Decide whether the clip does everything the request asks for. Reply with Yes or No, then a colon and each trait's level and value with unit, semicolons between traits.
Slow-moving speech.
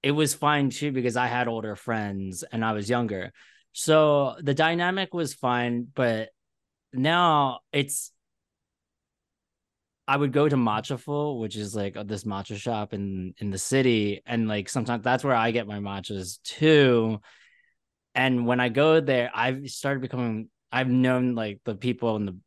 No: average, 165 wpm